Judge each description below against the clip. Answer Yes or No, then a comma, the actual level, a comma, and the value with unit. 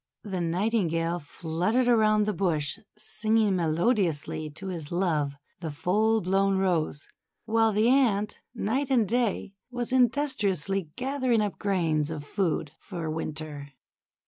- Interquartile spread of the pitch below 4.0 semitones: No, wide, 5.5 semitones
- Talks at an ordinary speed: No, slow, 130 wpm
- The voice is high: Yes, high, 195 Hz